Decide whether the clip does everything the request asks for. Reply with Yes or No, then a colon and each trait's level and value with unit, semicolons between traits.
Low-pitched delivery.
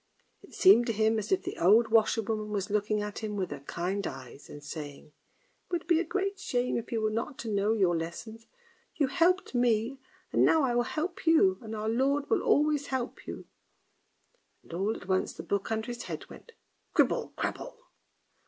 No: high, 225 Hz